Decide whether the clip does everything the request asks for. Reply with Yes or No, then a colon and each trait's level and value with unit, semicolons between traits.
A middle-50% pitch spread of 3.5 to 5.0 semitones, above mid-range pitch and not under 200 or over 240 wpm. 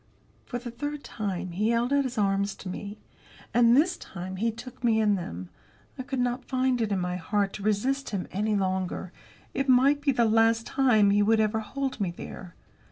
Yes: average, 4.2 semitones; high, 220 Hz; fast, 205 wpm